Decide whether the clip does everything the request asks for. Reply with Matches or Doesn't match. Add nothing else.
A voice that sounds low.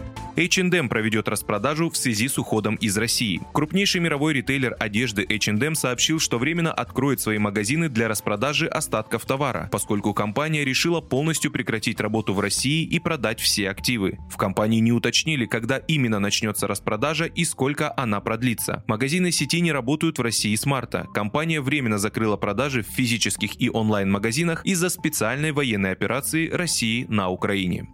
Matches